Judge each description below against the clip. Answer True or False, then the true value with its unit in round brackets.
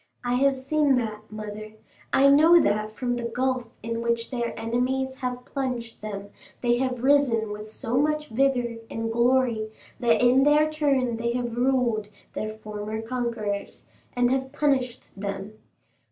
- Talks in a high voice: True (240 Hz)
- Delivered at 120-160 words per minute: True (155 wpm)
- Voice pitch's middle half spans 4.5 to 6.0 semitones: False (3.1 semitones)